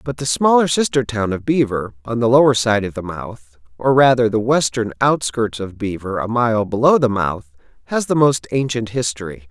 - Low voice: Yes, low, 115 Hz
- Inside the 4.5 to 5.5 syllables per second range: Yes, 5.0 syllables/s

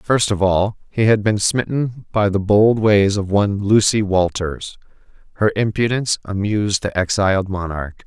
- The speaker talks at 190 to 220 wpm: No, average, 155 wpm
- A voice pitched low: Yes, low, 100 Hz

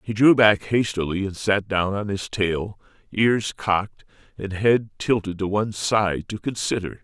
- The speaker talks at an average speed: Yes, average, 170 wpm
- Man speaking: Yes, male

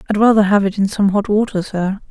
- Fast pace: Yes, fast, 255 wpm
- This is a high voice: Yes, high, 205 Hz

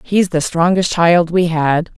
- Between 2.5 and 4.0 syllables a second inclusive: Yes, 3.8 syllables/s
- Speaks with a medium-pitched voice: Yes, medium, 170 Hz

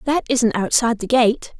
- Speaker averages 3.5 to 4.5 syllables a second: No, 5.1 syllables/s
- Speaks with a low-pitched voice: No, high, 235 Hz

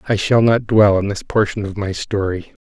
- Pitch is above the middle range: No, low, 105 Hz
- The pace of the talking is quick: Yes, fast, 225 wpm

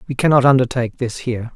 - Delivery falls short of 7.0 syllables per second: No, 7.2 syllables/s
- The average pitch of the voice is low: Yes, low, 125 Hz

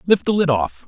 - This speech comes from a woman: No, male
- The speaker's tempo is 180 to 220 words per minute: No, fast, 275 wpm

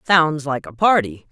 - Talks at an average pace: Yes, average, 185 wpm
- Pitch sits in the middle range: Yes, medium, 150 Hz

